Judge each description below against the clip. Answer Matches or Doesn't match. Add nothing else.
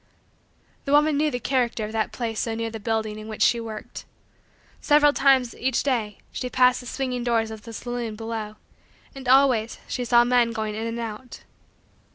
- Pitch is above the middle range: Matches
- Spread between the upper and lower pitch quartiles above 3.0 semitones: Doesn't match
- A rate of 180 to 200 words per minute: Matches